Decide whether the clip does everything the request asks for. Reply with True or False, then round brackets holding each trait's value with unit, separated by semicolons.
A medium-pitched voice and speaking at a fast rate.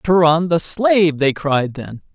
False (160 Hz; 170 wpm)